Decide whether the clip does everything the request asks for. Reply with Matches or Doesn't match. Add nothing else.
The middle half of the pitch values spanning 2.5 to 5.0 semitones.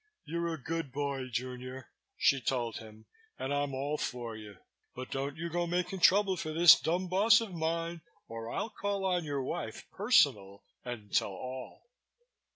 Doesn't match